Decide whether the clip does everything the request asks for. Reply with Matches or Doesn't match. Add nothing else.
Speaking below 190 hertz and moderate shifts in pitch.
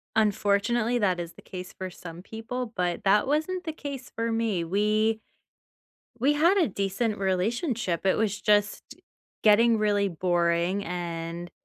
Doesn't match